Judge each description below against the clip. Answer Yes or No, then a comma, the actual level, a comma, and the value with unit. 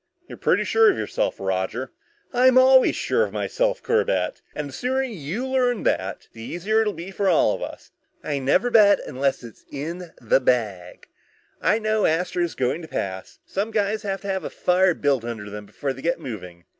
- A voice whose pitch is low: No, medium, 175 Hz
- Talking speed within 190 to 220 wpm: Yes, average, 195 wpm